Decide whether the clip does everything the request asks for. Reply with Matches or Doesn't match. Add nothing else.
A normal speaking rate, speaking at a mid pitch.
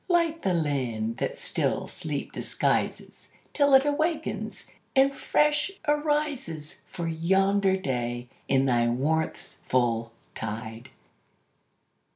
Doesn't match